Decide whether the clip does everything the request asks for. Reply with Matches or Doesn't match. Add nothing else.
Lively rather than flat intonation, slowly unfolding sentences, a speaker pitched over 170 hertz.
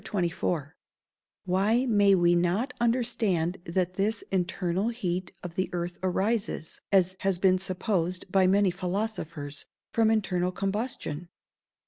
Doesn't match